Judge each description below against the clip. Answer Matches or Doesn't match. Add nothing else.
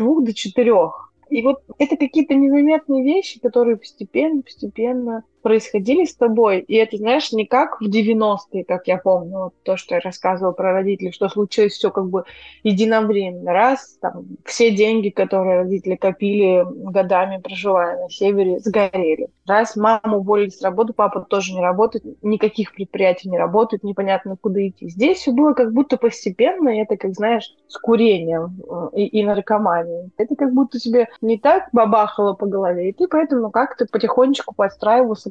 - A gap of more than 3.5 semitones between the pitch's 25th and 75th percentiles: Matches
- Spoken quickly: Matches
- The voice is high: Matches